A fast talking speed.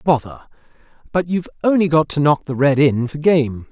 No: average, 195 wpm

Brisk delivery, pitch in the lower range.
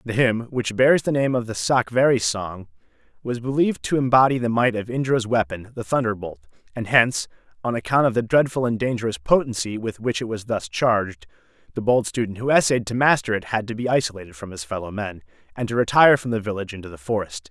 Yes: fast, 210 wpm; low, 115 Hz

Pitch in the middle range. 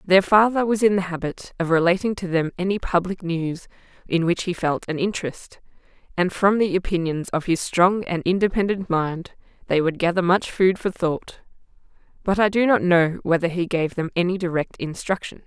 Yes: medium, 180 Hz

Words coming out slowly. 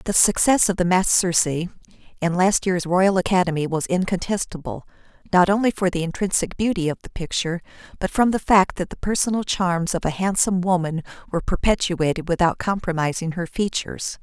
No: average, 170 wpm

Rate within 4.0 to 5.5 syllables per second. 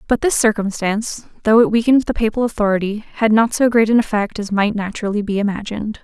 No: 6.3 syllables/s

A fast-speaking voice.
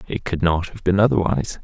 Yes: fast, 220 wpm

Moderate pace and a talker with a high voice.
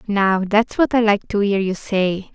No: fast, 230 wpm; high, 205 Hz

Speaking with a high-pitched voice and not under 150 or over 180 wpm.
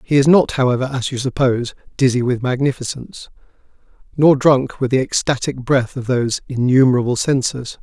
No: low, 130 Hz; average, 155 wpm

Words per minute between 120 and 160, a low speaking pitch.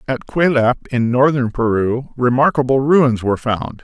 Yes: average, 140 wpm; low, 130 Hz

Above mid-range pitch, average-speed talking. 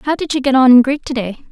No: very high, 260 Hz; fast, 315 wpm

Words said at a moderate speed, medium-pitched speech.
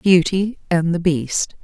Yes: average, 145 wpm; medium, 175 Hz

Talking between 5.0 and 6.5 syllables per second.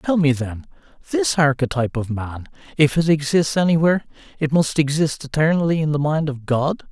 Yes: 5.5 syllables/s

